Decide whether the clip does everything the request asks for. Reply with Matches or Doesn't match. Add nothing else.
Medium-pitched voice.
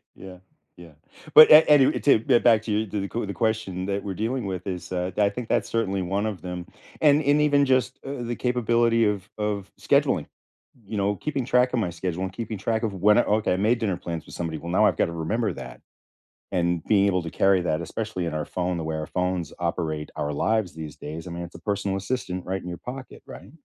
Doesn't match